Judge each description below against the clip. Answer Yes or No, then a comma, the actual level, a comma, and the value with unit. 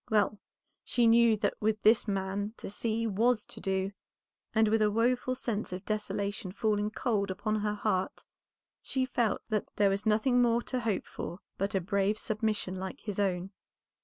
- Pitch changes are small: Yes, narrow, 2.3 semitones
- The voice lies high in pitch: Yes, high, 210 Hz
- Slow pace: No, average, 175 wpm